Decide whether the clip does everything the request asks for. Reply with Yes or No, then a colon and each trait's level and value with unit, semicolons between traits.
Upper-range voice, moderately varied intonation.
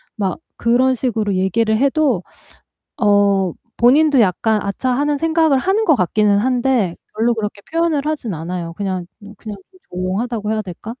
Yes: high, 220 Hz; average, 5.0 semitones